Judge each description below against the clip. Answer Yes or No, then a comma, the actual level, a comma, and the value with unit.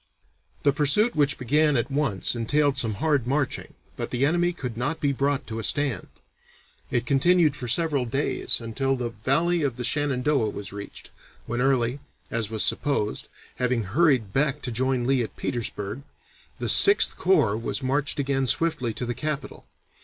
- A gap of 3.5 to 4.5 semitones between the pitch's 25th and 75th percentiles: Yes, average, 3.8 semitones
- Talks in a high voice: No, low, 135 Hz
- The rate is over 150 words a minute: Yes, average, 170 wpm